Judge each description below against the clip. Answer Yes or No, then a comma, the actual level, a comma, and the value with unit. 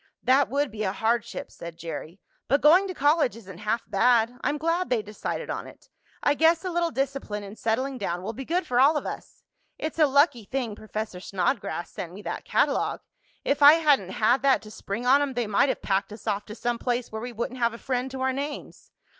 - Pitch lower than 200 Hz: No, high, 245 Hz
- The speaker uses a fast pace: Yes, fast, 225 wpm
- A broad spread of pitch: No, average, 5.0 semitones